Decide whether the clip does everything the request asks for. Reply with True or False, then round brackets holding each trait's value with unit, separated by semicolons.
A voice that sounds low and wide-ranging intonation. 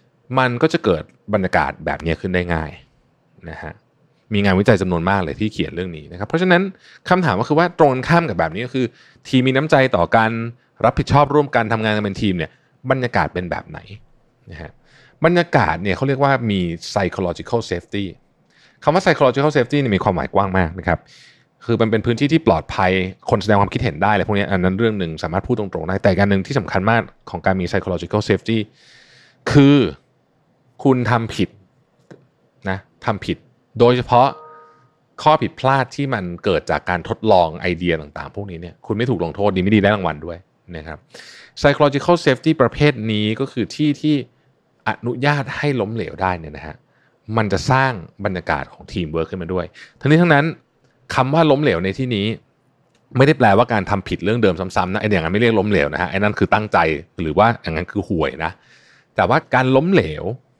True (110 Hz; 6.0 semitones)